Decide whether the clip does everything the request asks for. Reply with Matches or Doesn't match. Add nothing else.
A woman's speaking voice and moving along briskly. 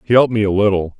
Doesn't match